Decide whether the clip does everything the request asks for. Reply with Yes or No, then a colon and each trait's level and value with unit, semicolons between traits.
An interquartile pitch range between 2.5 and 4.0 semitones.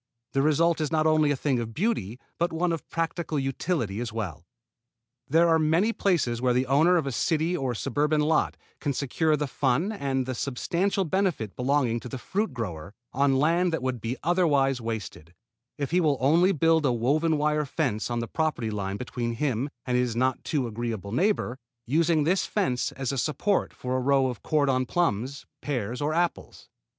No: average, 4.8 semitones